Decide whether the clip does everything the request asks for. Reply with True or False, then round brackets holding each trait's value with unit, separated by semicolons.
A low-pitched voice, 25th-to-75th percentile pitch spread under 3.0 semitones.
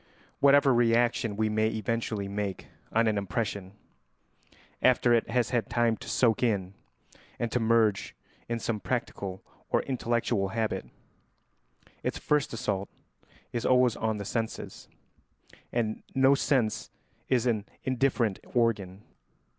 True (115 Hz; 2.6 semitones)